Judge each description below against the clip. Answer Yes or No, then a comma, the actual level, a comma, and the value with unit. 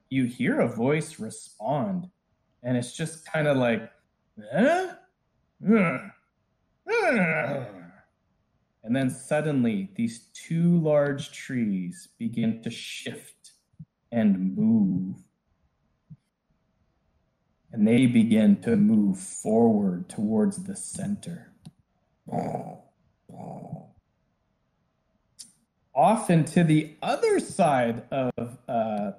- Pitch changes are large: Yes, wide, 8.5 semitones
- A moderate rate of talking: No, slow, 85 wpm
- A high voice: No, medium, 180 Hz